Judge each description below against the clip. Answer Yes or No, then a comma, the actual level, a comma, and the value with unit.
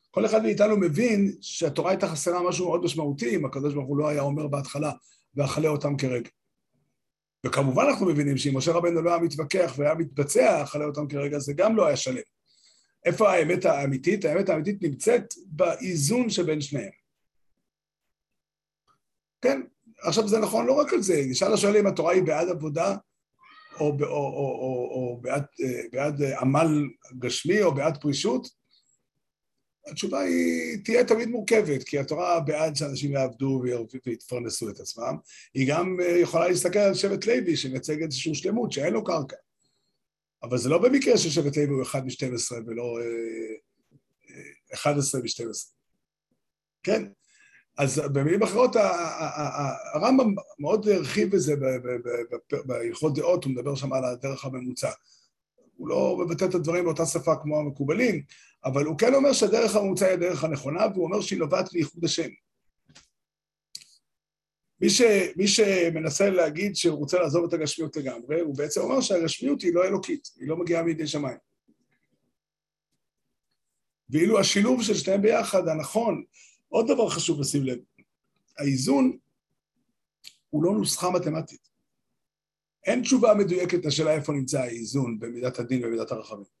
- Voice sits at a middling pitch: Yes, medium, 160 Hz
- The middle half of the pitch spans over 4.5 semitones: Yes, wide, 5.6 semitones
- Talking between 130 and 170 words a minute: Yes, average, 145 wpm